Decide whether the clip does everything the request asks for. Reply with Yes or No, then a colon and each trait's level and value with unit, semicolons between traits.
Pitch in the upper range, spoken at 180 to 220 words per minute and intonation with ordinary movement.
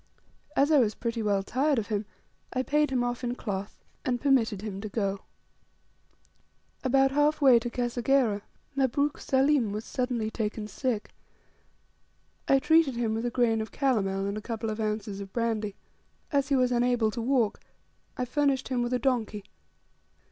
No: high, 240 Hz; average, 170 wpm; average, 3.7 semitones